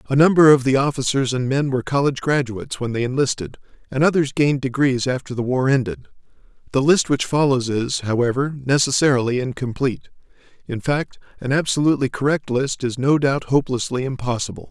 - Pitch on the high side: No, low, 135 Hz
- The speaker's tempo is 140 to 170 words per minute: Yes, average, 165 wpm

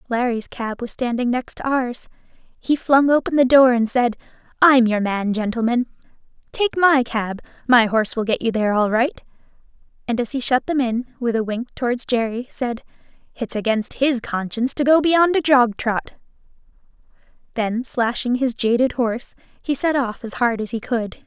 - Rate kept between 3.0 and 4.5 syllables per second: No, 5.0 syllables/s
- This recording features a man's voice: No, female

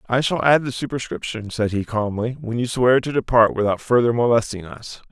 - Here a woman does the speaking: No, male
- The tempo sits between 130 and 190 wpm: No, average, 200 wpm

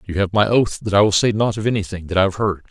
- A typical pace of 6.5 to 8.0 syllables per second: Yes, 6.9 syllables/s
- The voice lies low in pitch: Yes, low, 100 Hz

